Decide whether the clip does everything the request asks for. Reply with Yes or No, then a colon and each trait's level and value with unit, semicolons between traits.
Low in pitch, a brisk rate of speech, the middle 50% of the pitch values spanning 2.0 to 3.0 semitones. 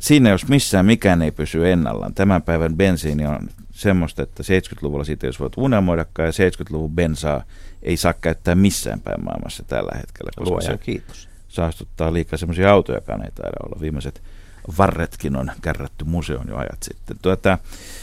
No: very low, 85 Hz; fast, 160 wpm; average, 3.5 semitones